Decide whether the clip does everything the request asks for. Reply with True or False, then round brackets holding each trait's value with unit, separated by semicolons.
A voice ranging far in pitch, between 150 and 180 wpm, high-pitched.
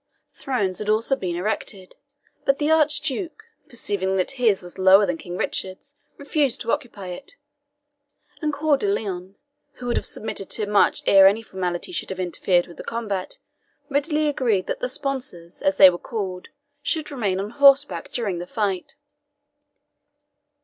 True (6.7 semitones; 160 wpm; 210 Hz)